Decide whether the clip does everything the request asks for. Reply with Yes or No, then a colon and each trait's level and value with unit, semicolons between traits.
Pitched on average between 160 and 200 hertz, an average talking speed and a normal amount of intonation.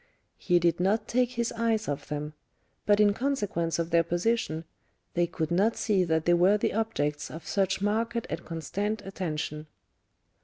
Yes: high, 190 Hz; average, 165 wpm; average, 4.8 semitones